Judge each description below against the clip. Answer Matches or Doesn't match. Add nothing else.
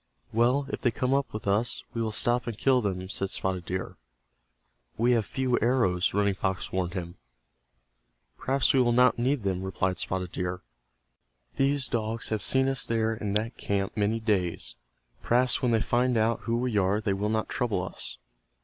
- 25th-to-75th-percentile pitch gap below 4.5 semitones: Matches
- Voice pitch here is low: Matches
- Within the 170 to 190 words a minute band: Matches